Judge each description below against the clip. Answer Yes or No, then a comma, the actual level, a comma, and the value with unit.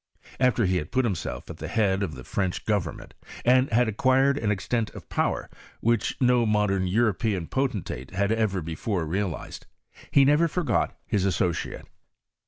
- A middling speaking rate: Yes, average, 165 wpm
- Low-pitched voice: Yes, low, 105 Hz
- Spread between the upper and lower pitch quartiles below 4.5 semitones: No, average, 4.8 semitones